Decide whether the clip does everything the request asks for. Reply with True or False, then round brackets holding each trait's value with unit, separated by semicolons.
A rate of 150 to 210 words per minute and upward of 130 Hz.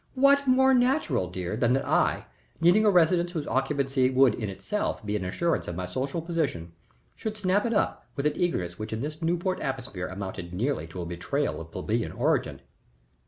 True (190 wpm; 140 Hz)